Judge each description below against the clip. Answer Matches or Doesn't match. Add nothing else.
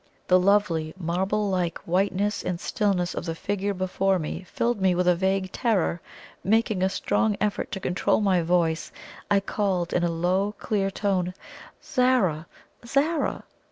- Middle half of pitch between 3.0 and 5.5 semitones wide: Doesn't match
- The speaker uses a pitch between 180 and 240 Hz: Matches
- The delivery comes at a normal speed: Matches